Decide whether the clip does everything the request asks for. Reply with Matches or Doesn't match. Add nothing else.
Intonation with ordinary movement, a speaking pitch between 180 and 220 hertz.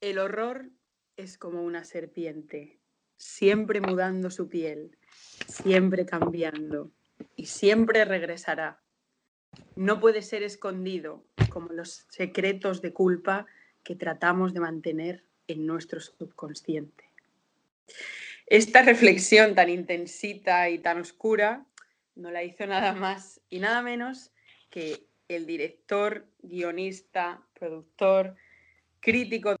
Matches